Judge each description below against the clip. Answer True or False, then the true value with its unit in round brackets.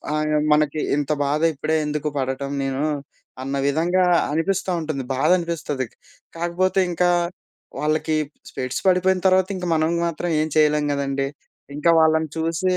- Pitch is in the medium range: True (155 Hz)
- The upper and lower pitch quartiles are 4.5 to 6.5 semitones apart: False (3.2 semitones)